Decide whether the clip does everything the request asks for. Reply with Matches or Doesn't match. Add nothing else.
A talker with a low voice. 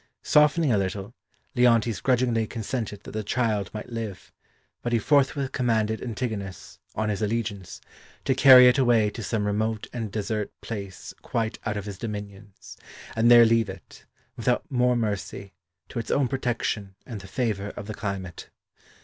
Matches